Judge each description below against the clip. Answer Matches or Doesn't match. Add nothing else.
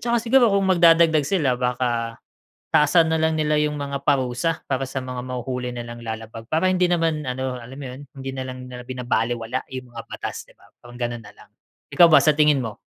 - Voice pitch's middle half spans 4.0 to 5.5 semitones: Matches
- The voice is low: Matches